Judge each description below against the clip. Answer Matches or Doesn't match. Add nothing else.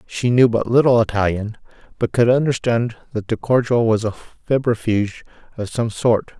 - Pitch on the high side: Doesn't match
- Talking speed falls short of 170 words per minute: Matches